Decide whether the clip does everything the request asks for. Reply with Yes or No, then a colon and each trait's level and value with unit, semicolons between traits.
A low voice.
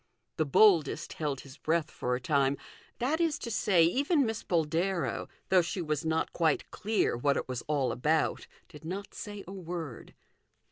No: medium, 165 Hz